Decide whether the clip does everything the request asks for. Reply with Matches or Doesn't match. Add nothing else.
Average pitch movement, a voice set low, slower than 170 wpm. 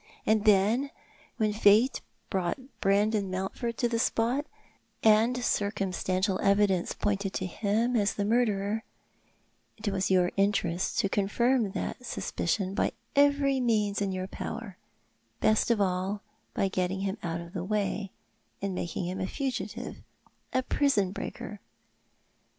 Doesn't match